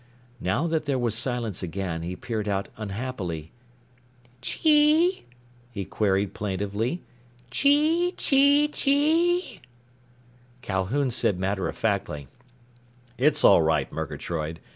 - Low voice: Yes, low, 115 Hz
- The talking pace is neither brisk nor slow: No, slow, 105 wpm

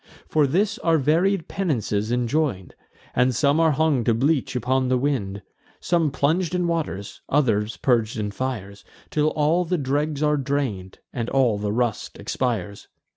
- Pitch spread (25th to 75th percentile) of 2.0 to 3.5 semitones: No, wide, 5.4 semitones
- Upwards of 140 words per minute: Yes, average, 155 wpm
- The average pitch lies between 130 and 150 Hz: Yes, low, 135 Hz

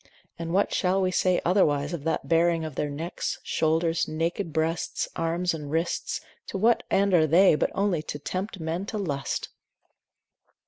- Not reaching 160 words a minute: No, average, 170 wpm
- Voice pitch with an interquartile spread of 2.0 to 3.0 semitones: Yes, average, 2.7 semitones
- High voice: No, medium, 165 Hz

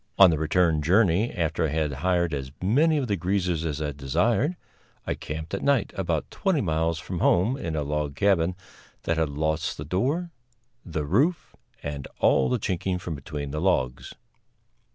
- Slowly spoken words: No, average, 175 wpm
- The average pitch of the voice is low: Yes, very low, 85 Hz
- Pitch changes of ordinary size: Yes, average, 4.3 semitones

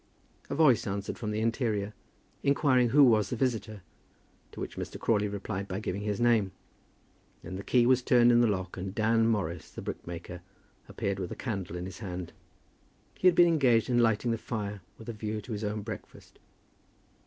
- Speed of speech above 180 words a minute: Yes, average, 190 wpm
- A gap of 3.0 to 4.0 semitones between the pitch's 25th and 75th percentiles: Yes, average, 3.3 semitones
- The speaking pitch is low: Yes, low, 110 Hz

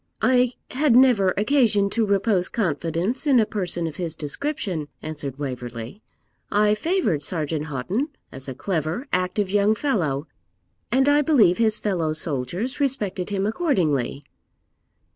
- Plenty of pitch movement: Yes, wide, 7.2 semitones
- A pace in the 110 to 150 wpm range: Yes, slow, 135 wpm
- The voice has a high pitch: Yes, high, 195 Hz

